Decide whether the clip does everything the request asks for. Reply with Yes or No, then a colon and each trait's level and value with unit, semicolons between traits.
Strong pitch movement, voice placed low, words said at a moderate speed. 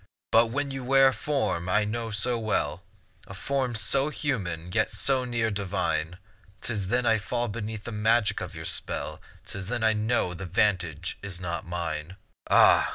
No: average, 4.7 semitones; low, 110 Hz; average, 175 wpm